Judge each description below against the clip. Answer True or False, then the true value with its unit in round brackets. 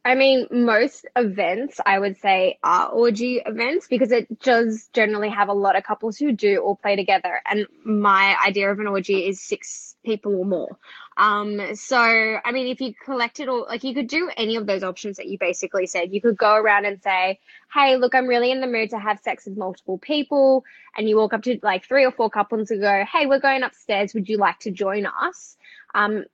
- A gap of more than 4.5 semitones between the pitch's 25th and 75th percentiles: False (3.9 semitones)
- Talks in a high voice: True (220 Hz)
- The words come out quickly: True (225 wpm)